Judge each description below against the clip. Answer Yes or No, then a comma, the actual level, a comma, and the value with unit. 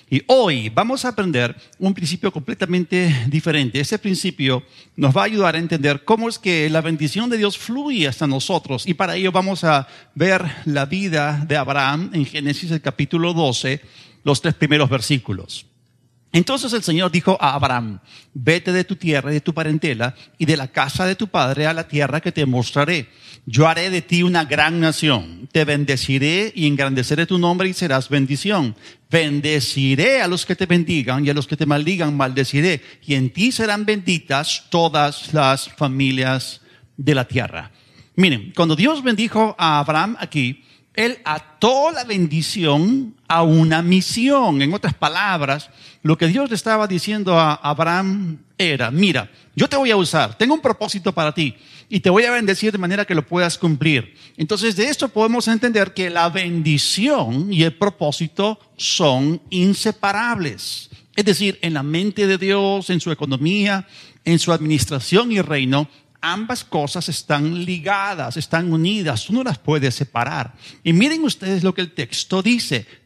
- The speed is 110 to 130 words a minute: No, average, 170 wpm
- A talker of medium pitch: Yes, medium, 160 Hz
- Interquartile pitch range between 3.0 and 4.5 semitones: No, average, 5.0 semitones